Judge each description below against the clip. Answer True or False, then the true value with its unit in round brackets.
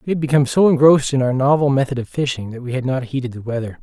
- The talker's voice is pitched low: True (130 Hz)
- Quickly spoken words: True (280 wpm)